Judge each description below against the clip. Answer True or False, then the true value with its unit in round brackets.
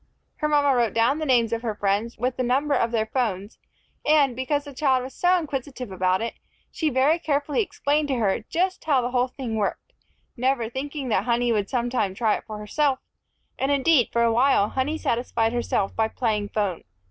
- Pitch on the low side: False (250 Hz)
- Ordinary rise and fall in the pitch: True (4.0 semitones)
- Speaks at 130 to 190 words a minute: False (200 wpm)